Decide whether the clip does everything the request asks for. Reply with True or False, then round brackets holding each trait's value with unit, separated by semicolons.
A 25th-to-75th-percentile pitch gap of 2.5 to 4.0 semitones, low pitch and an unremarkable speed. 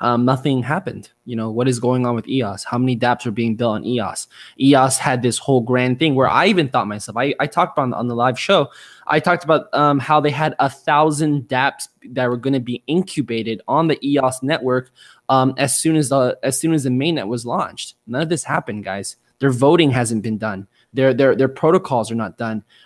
False (3.4 semitones; 130 Hz; 230 wpm)